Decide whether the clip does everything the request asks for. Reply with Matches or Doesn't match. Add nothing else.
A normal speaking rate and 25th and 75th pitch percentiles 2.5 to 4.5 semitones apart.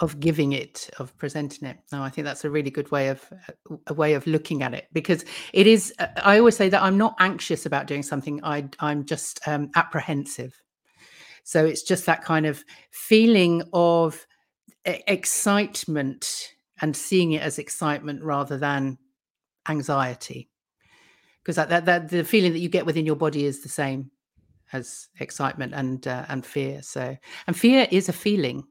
Matches